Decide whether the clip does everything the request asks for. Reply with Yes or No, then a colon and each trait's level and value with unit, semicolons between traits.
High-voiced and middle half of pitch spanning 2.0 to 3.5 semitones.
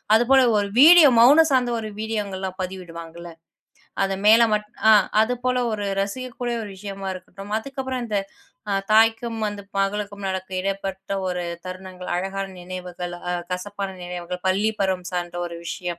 Yes: high, 195 Hz; average, 3.2 semitones